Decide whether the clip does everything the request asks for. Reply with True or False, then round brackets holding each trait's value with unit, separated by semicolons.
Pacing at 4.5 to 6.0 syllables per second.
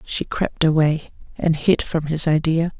False (4.1 syllables/s)